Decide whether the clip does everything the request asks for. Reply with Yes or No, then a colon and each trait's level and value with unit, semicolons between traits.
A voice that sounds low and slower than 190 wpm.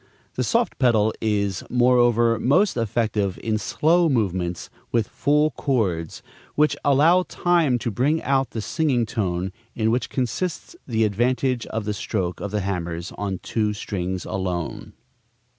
Yes: low, 115 Hz; average, 140 wpm